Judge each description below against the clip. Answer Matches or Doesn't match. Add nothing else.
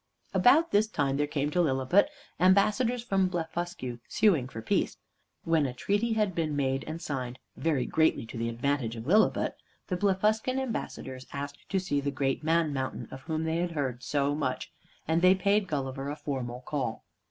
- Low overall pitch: Doesn't match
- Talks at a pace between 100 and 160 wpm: Doesn't match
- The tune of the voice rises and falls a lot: Matches